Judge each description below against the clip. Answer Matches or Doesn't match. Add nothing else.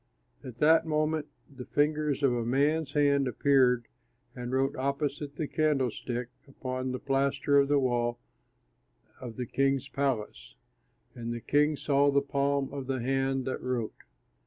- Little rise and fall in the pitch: Matches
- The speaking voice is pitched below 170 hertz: Matches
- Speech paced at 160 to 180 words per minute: Doesn't match